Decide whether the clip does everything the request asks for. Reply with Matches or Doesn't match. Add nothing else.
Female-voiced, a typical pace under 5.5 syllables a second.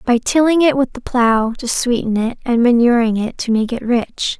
Matches